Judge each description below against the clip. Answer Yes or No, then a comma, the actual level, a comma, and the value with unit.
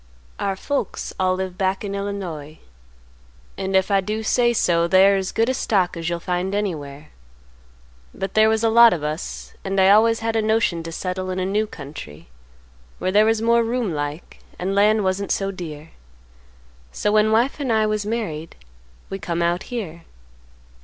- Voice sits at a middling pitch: No, high, 195 Hz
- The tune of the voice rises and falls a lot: No, average, 3.9 semitones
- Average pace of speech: Yes, average, 180 wpm